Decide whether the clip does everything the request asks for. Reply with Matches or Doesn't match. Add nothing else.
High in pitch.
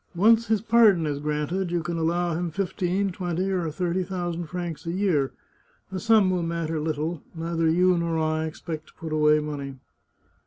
Doesn't match